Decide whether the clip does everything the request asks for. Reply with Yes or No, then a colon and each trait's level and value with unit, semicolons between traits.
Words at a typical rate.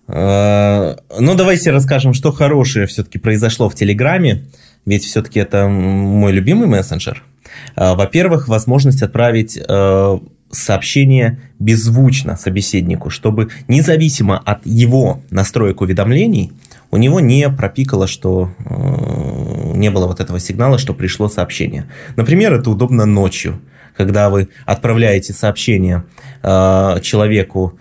No: slow, 105 wpm